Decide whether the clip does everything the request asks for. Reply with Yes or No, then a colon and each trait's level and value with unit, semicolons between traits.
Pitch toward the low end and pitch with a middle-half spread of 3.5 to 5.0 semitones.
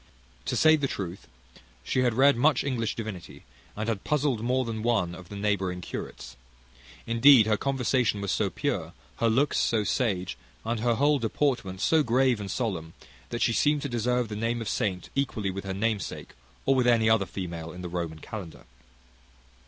Yes: low, 115 Hz; average, 4.7 semitones